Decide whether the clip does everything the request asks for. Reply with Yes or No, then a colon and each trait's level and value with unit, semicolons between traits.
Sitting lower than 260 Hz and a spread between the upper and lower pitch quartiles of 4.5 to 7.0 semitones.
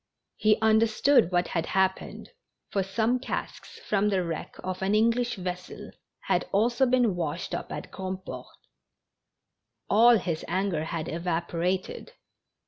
No: high, 190 Hz; average, 3.8 semitones